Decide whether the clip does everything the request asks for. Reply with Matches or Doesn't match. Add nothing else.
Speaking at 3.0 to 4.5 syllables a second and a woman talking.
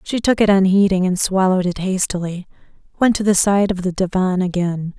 Doesn't match